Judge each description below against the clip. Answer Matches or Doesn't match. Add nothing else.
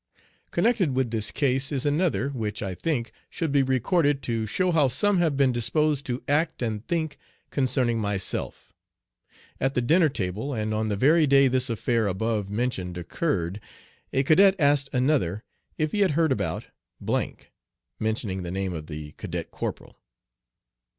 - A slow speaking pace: Doesn't match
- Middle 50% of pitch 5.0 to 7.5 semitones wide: Matches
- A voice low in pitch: Matches